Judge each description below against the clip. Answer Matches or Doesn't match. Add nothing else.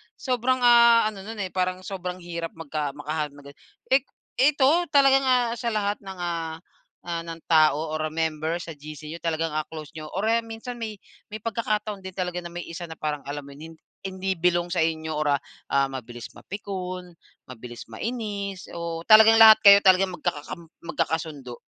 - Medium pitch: Matches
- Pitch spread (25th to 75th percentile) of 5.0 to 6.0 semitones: Matches